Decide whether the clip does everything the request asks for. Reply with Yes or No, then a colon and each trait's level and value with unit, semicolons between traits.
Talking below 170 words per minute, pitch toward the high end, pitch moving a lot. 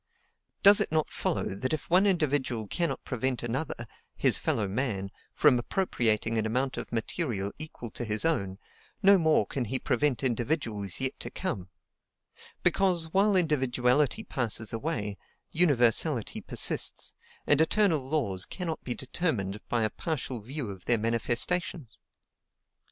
No: average, 140 wpm; low, 130 Hz; wide, 6.0 semitones